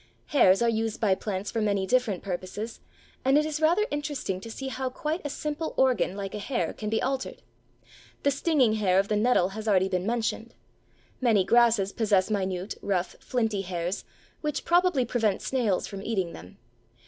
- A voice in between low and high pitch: No, high, 220 Hz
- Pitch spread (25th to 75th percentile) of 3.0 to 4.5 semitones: No, average, 5.2 semitones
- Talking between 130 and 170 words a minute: No, average, 180 wpm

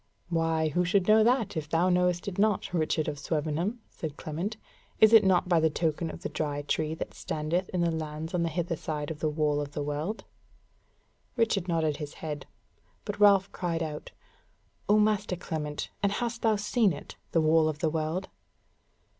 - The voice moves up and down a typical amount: Yes, average, 4.0 semitones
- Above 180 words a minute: Yes, average, 190 wpm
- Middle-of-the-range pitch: Yes, medium, 165 Hz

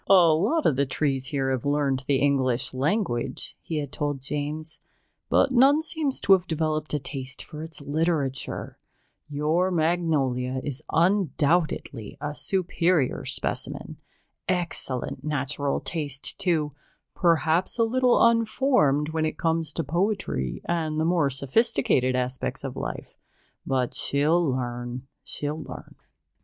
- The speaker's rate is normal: No, slow, 130 wpm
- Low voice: No, medium, 150 Hz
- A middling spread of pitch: Yes, average, 4.2 semitones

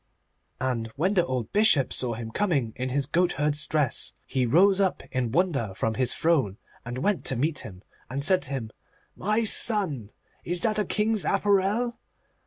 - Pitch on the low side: No, medium, 150 Hz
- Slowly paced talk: No, average, 175 wpm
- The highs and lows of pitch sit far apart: Yes, wide, 7.5 semitones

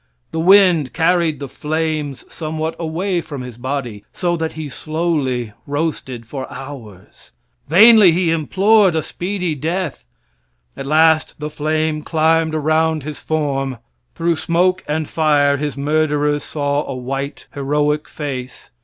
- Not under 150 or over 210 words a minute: No, slow, 135 wpm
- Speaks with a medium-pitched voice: Yes, medium, 155 Hz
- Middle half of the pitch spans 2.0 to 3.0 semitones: Yes, narrow, 2.5 semitones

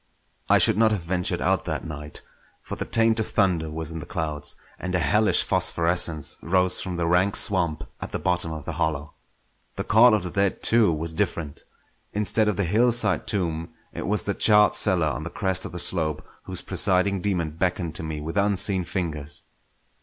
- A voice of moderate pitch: No, very low, 90 Hz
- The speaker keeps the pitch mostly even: No, average, 3.9 semitones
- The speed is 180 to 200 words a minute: Yes, average, 195 wpm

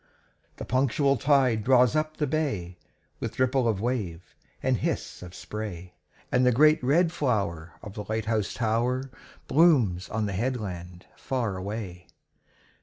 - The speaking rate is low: No, average, 145 wpm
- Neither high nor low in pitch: No, low, 115 Hz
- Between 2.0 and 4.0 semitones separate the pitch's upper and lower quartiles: No, average, 5.3 semitones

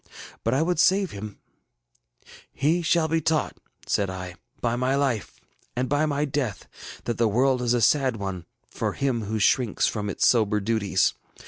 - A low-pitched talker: Yes, low, 125 Hz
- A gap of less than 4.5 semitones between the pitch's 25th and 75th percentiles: No, wide, 5.4 semitones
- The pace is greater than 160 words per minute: Yes, average, 175 wpm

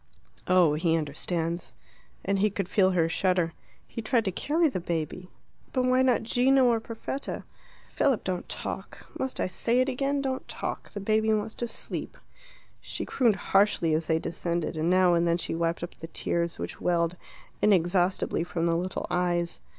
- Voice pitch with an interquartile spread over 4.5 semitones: Yes, average, 5.1 semitones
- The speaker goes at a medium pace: Yes, average, 180 wpm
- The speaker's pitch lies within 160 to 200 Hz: Yes, medium, 185 Hz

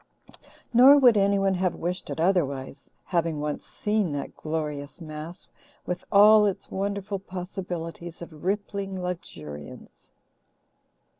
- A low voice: No, medium, 180 Hz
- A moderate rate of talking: No, slow, 115 wpm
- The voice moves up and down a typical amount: Yes, average, 4.0 semitones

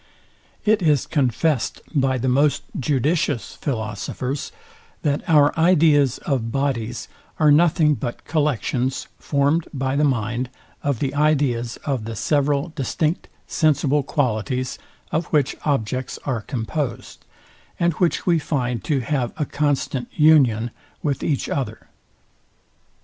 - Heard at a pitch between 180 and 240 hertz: No, medium, 140 Hz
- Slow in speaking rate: Yes, slow, 120 wpm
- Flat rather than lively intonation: No, average, 3.3 semitones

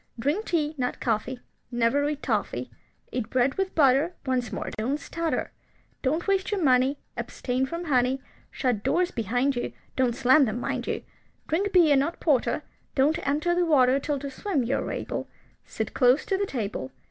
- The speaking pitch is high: Yes, very high, 275 Hz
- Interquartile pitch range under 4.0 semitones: No, average, 4.3 semitones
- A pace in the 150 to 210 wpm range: Yes, average, 175 wpm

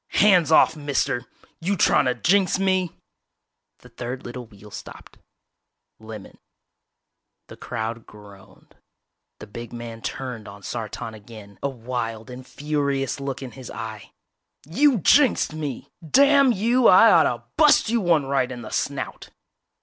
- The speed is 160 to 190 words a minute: No, average, 140 wpm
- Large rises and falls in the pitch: Yes, wide, 7.6 semitones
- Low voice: Yes, low, 130 Hz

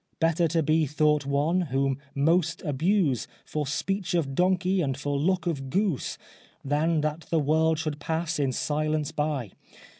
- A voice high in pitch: No, medium, 155 Hz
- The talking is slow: No, average, 155 wpm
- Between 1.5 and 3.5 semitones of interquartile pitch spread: Yes, average, 2.8 semitones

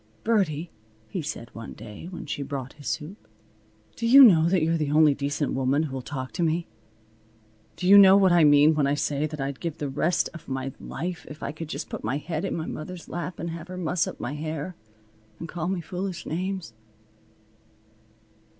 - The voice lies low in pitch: No, medium, 160 Hz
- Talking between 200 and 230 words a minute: Yes, fast, 205 wpm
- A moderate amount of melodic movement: Yes, average, 3.6 semitones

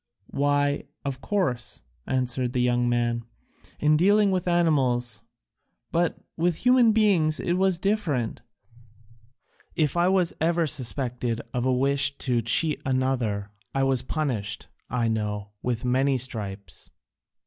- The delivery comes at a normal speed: No, slow, 125 wpm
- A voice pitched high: No, low, 135 Hz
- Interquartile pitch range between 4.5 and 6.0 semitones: Yes, wide, 5.5 semitones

